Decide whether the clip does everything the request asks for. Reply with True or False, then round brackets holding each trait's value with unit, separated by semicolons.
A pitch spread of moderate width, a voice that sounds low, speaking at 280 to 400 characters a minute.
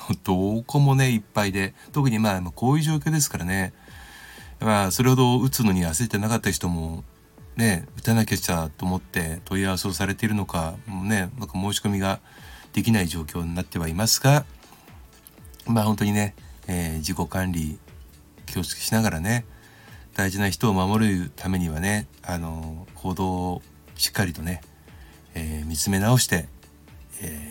True (4.5 semitones; 95 Hz; 320 characters per minute)